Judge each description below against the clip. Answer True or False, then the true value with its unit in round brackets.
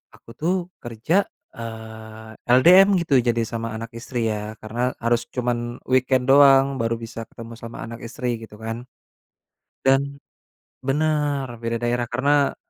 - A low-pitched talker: True (120 Hz)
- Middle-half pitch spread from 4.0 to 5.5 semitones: False (2.8 semitones)